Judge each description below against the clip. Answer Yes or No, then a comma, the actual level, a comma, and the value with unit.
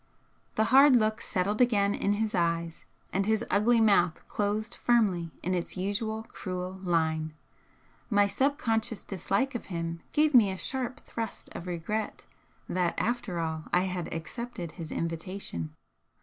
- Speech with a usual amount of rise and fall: Yes, average, 4.5 semitones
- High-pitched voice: Yes, high, 200 Hz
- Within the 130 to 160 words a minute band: Yes, average, 145 wpm